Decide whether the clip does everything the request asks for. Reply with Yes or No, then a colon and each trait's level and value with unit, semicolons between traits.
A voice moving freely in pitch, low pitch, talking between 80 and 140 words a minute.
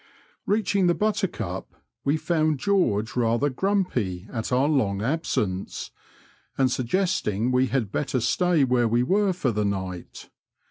Yes: wide, 8.3 semitones; low, 130 Hz; slow, 135 wpm